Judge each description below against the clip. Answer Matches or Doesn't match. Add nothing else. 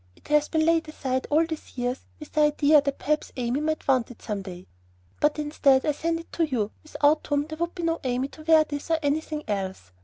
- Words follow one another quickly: Matches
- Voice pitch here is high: Matches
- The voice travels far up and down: Doesn't match